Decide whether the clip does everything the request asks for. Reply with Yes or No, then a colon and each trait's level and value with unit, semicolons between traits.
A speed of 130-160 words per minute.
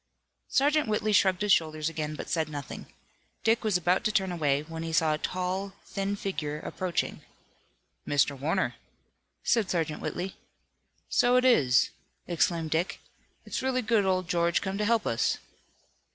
Yes: average, 155 wpm